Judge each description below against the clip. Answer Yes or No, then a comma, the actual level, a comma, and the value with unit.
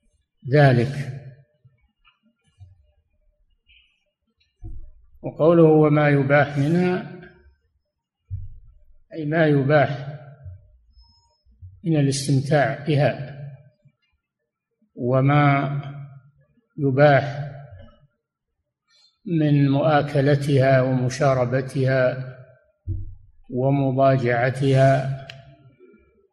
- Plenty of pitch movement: Yes, wide, 6.6 semitones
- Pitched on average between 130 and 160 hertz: Yes, low, 135 Hz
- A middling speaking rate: No, slow, 40 wpm